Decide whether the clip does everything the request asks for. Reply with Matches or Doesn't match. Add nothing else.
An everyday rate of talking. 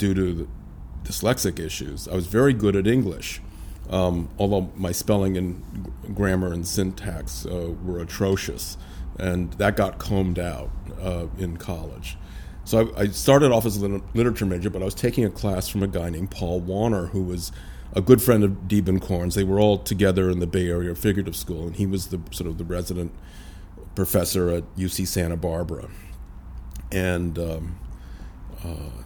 Matches